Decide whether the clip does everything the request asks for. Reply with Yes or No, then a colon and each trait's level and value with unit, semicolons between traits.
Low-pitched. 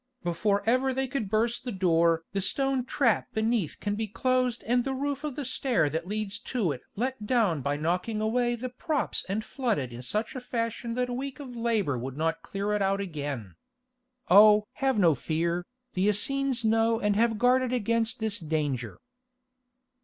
No: high, 220 Hz